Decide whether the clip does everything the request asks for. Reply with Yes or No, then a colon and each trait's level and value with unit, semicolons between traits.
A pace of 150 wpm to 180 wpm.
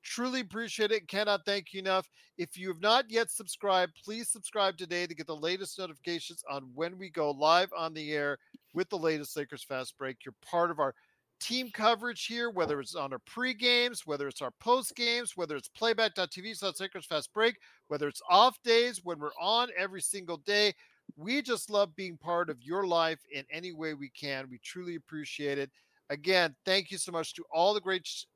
No: average, 200 wpm